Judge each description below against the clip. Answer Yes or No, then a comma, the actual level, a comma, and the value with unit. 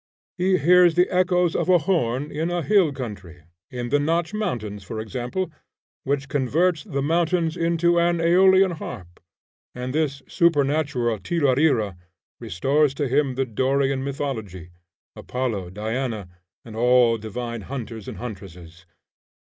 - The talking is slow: Yes, slow, 130 wpm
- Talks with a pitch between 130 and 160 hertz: Yes, low, 135 Hz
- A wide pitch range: Yes, wide, 6.4 semitones